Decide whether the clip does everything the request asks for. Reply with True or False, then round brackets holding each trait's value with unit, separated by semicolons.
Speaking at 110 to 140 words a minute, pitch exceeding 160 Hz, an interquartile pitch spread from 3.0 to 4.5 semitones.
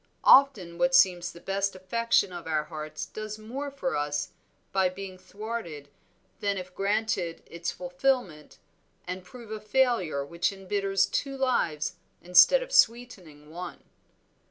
False (135 wpm; 190 Hz; 5.2 semitones)